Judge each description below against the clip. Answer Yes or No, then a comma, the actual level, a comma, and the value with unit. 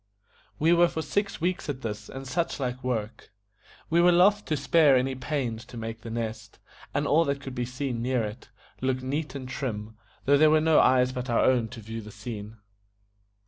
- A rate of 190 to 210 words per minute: Yes, fast, 205 wpm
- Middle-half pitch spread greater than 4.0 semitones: Yes, average, 4.5 semitones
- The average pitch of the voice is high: No, low, 130 Hz